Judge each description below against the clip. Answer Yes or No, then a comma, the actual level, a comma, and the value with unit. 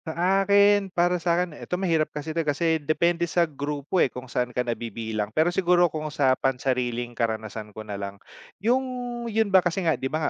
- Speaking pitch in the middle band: Yes, medium, 155 Hz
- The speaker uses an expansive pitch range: Yes, wide, 6.1 semitones